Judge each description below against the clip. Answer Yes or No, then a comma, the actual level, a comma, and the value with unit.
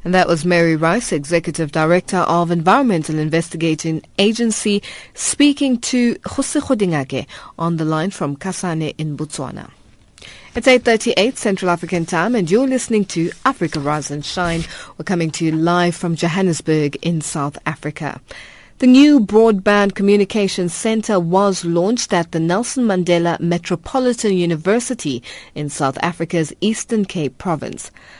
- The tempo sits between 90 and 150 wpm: Yes, slow, 135 wpm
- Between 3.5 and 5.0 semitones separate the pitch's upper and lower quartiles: Yes, average, 4.6 semitones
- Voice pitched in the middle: Yes, medium, 175 Hz